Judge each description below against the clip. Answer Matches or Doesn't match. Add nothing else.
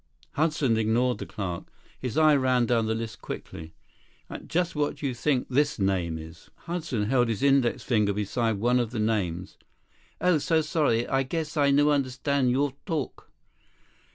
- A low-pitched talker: Matches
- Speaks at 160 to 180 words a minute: Matches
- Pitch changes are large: Doesn't match